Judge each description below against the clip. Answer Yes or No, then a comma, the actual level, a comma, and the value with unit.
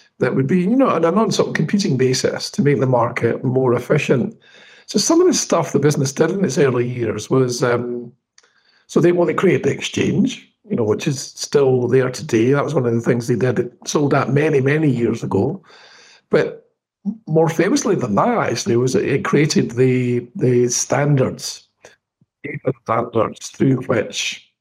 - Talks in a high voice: No, low, 135 Hz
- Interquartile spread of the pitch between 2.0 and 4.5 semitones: No, average, 5.2 semitones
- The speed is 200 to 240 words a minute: No, average, 185 wpm